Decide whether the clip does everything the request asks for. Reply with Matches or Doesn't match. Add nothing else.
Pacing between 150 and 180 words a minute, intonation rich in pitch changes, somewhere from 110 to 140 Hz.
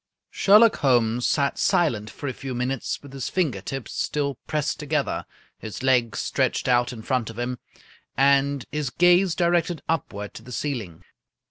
Doesn't match